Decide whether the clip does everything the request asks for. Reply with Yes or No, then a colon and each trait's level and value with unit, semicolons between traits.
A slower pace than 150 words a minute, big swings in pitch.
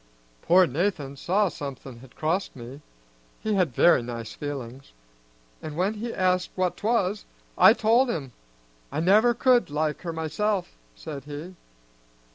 Yes: average, 140 wpm; wide, 6.5 semitones